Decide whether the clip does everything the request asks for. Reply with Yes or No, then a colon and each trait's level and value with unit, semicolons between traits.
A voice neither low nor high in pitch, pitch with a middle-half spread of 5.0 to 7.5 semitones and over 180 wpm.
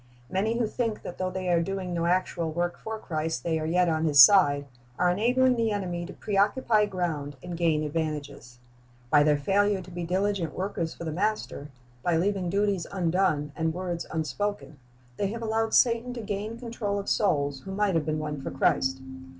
No: medium, 180 Hz; average, 4.3 semitones; average, 195 wpm